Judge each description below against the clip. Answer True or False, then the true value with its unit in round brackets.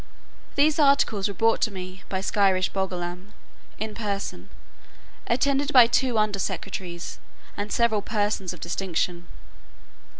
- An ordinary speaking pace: False (125 wpm)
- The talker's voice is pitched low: False (205 Hz)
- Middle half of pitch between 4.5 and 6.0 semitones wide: False (3.8 semitones)